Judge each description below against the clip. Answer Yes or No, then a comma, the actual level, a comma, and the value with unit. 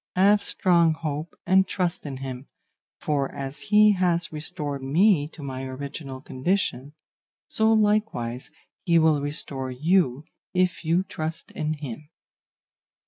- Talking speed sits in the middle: No, slow, 130 wpm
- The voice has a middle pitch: Yes, medium, 155 Hz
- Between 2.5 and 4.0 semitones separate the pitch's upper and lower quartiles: No, average, 4.8 semitones